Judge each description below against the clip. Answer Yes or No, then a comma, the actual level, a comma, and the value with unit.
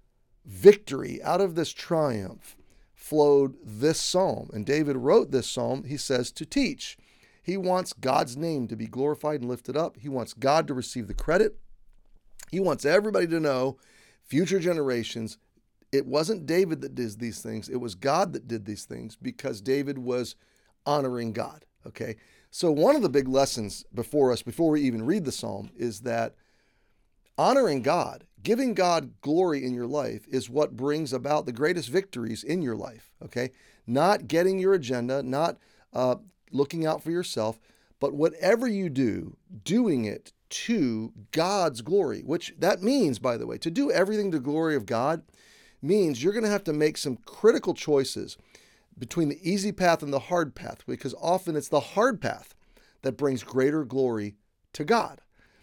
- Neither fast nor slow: Yes, average, 170 wpm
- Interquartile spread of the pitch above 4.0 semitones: Yes, average, 5.2 semitones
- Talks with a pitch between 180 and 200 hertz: No, medium, 140 Hz